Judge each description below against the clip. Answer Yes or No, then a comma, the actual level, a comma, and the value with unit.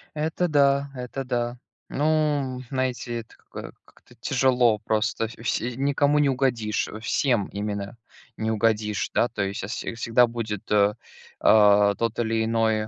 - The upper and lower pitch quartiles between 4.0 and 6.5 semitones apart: No, average, 3.6 semitones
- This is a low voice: Yes, low, 115 Hz